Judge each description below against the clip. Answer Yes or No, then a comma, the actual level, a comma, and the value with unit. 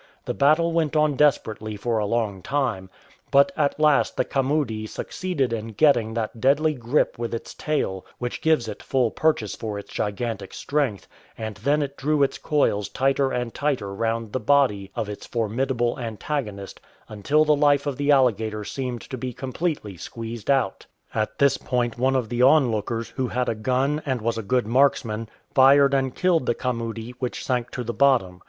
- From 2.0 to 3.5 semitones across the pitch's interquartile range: No, average, 4.0 semitones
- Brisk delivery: No, average, 180 wpm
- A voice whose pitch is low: Yes, low, 125 Hz